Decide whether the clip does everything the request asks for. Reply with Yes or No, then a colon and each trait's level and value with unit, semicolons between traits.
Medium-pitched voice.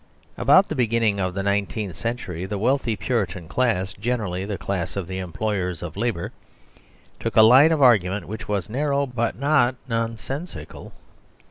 No: low, 110 Hz